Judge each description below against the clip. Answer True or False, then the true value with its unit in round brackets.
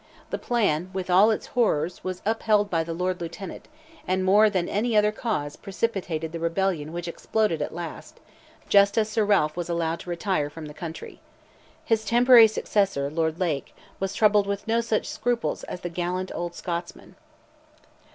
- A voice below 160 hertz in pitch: False (185 Hz)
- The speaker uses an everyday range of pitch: True (4.0 semitones)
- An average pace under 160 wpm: False (170 wpm)